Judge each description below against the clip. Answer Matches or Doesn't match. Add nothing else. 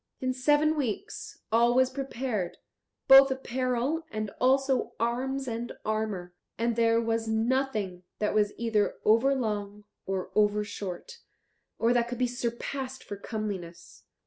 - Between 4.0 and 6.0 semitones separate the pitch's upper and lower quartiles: Doesn't match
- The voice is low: Doesn't match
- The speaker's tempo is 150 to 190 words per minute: Doesn't match